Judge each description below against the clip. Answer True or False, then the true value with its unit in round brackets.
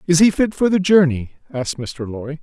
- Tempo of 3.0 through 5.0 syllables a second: False (5.8 syllables/s)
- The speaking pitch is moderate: True (155 Hz)